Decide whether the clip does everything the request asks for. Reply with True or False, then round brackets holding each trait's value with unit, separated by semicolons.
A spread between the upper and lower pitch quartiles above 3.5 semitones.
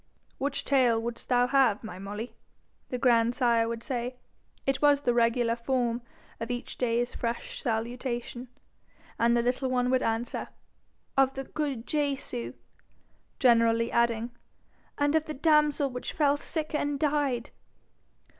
False (3.0 semitones)